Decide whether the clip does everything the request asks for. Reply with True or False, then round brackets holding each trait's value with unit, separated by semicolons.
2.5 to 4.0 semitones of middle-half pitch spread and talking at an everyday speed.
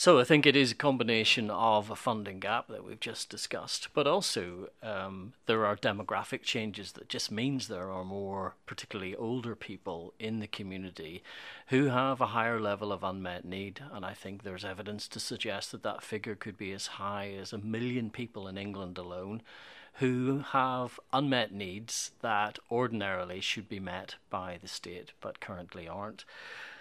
True (3.6 semitones; 175 wpm)